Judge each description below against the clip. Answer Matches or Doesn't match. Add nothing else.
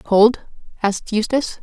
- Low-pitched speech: Doesn't match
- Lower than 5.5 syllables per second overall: Matches